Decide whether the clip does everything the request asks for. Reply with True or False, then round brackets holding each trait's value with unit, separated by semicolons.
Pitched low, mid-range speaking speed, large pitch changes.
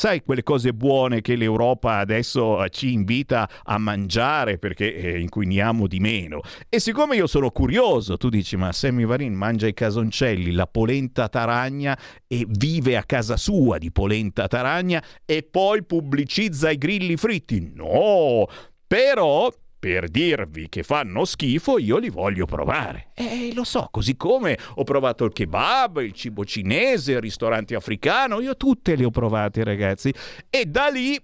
True (120 Hz; 155 wpm; 6.2 semitones)